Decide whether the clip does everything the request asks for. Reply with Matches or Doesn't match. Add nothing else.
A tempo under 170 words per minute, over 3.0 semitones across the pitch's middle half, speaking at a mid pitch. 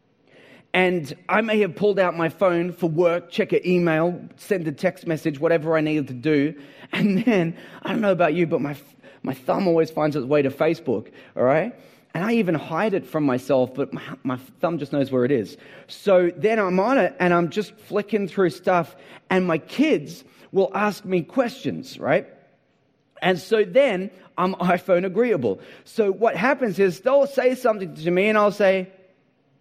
Doesn't match